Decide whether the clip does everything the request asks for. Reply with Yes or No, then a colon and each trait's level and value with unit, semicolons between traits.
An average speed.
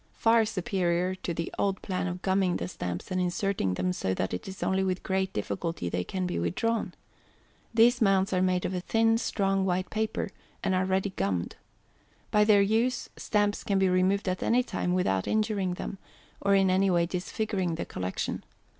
Yes: average, 190 wpm